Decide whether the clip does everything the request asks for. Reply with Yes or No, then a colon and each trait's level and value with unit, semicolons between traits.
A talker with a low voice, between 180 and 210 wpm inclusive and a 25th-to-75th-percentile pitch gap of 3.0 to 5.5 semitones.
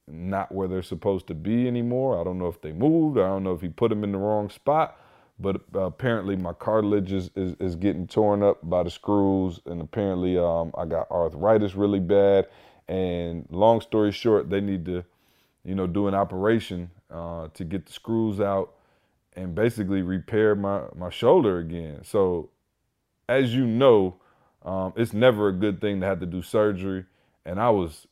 No: very low, 95 Hz; average, 190 wpm; narrow, 2.6 semitones